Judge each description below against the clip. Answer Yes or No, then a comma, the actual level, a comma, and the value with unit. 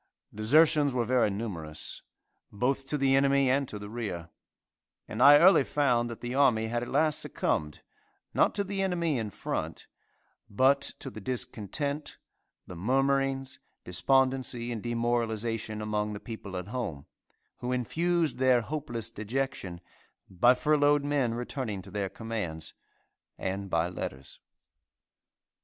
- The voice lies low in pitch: Yes, low, 120 Hz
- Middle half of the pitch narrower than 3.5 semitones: No, average, 4.5 semitones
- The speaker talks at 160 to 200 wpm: No, slow, 135 wpm